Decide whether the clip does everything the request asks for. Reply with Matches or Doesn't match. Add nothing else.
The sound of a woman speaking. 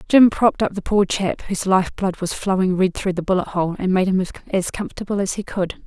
Matches